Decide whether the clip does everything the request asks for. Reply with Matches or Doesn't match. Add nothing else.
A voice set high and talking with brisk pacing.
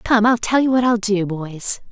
Matches